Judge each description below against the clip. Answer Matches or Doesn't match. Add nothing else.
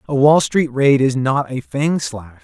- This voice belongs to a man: Matches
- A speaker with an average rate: Doesn't match